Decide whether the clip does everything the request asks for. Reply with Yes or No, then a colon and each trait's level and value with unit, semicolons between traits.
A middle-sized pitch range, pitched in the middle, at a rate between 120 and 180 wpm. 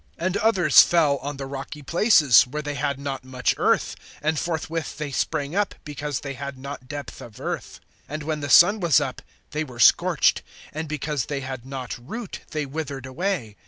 No: average, 3.0 semitones; medium, 145 Hz; average, 190 wpm